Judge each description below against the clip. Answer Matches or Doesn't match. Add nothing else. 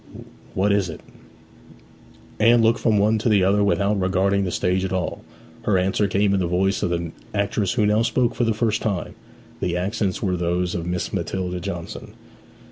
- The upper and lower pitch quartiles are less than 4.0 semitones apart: Matches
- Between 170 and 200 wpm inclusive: Matches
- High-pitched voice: Doesn't match